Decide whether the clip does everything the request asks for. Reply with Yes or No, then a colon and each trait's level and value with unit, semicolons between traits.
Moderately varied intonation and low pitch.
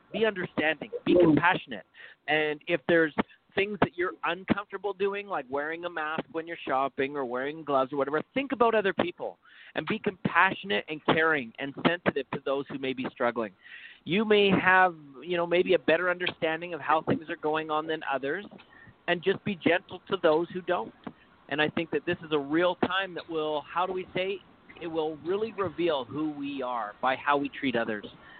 No: average, 4.3 semitones; medium, 165 Hz